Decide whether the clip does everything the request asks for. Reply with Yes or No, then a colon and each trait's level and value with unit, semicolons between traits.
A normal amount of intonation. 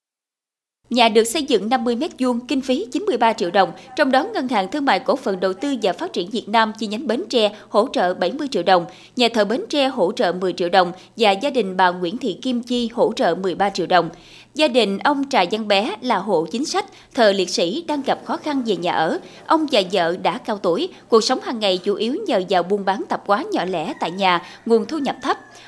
No: wide, 5.9 semitones